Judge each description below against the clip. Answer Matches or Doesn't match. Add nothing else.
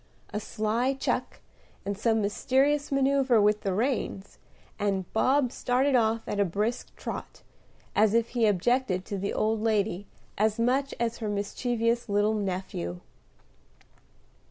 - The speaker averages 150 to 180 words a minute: Doesn't match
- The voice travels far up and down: Doesn't match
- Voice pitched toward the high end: Matches